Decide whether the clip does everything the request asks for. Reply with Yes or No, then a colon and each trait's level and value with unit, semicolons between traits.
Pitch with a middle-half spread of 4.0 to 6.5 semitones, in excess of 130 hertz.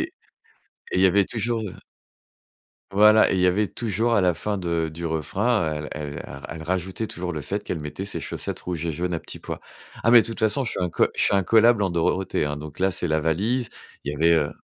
No: average, 4.7 semitones; very low, 90 Hz